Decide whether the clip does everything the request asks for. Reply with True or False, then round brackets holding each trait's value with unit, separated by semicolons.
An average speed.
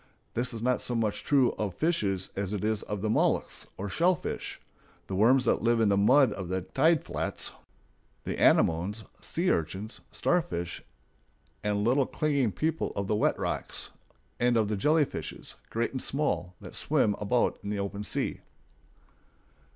True (165 wpm)